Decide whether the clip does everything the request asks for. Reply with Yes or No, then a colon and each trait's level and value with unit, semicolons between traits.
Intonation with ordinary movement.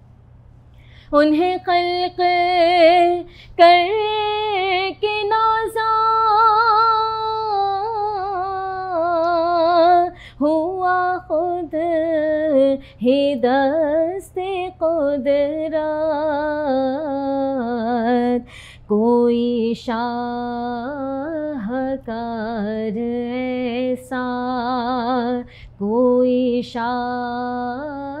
No: wide, 6.5 semitones